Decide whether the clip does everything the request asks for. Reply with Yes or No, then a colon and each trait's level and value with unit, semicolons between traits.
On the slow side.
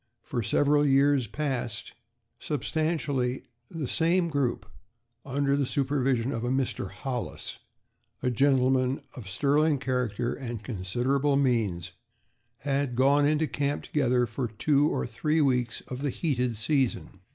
Yes: slow, 130 wpm